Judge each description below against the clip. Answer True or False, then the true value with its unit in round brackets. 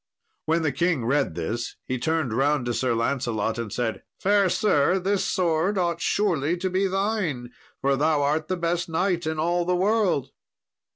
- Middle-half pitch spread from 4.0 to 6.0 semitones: True (5.3 semitones)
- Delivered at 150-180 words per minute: True (175 wpm)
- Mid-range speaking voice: True (160 Hz)